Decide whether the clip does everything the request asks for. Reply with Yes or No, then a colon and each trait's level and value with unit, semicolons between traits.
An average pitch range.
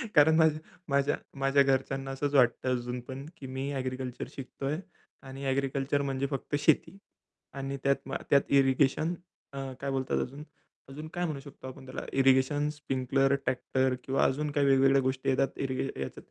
No: narrow, 1.2 semitones